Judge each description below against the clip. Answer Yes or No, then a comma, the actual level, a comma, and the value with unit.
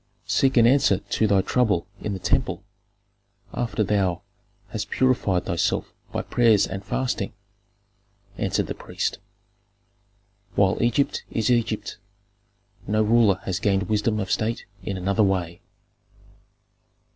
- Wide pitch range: No, average, 3.2 semitones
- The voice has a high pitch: No, low, 105 Hz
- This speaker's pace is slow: Yes, slow, 120 wpm